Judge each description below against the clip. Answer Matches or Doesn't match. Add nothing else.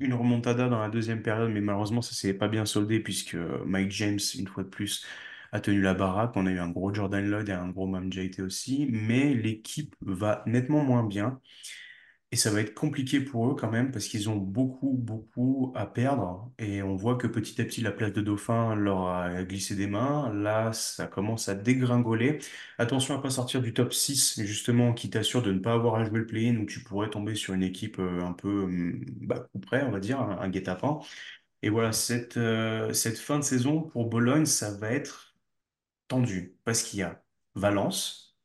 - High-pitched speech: Doesn't match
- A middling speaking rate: Matches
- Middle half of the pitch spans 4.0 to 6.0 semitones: Doesn't match